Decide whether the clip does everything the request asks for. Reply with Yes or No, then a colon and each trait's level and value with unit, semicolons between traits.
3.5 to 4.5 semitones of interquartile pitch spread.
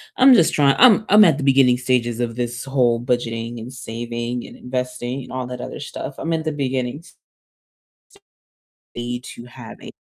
No: narrow, 2.4 semitones